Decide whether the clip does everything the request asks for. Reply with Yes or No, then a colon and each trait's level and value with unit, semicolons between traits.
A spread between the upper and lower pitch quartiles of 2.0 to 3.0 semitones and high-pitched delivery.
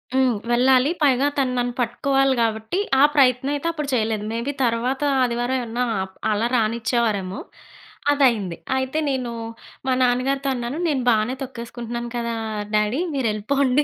Yes: average, 2.7 semitones; high, 245 Hz